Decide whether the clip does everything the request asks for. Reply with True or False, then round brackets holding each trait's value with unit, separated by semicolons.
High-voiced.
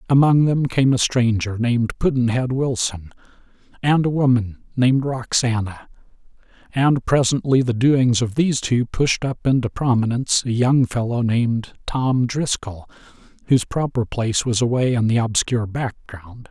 False (125 Hz)